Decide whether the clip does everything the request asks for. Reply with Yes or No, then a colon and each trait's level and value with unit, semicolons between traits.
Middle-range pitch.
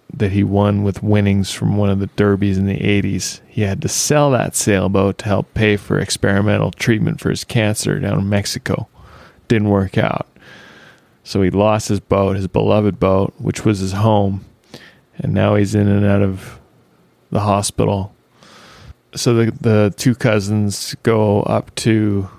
No: low, 100 Hz